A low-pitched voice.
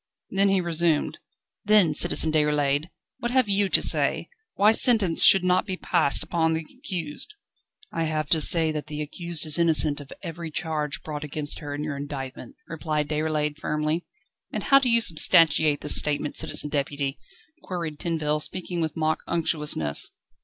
No: medium, 155 Hz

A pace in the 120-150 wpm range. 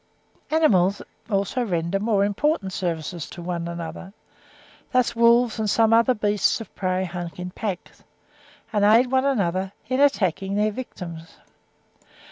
Yes: slow, 135 wpm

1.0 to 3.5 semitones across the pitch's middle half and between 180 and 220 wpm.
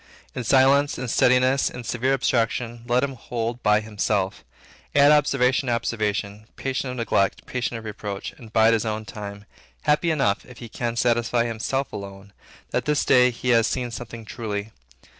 No: average, 2.9 semitones; average, 170 wpm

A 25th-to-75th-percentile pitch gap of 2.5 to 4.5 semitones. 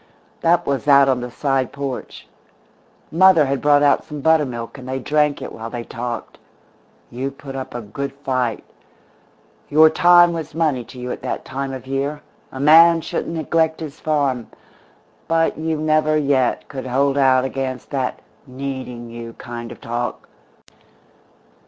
Yes: average, 3.2 semitones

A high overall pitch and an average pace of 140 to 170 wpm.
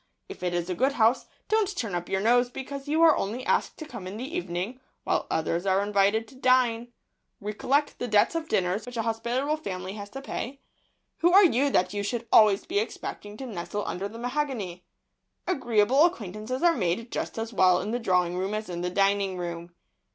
No: high, 225 Hz; fast, 205 wpm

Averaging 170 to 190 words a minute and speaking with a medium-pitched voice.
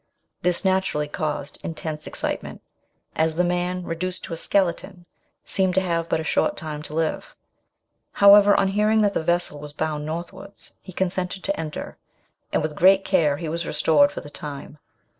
Yes: average, 175 wpm; medium, 170 Hz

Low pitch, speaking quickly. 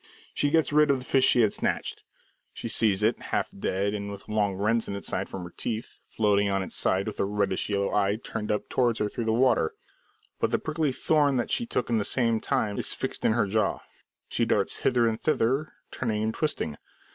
Yes: low, 110 Hz; fast, 230 wpm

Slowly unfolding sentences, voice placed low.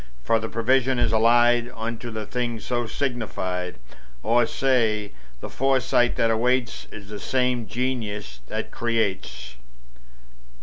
Yes: slow, 125 wpm; low, 115 Hz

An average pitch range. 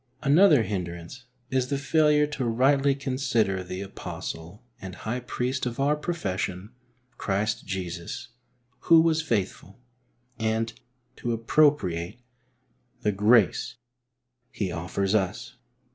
No: wide, 6.5 semitones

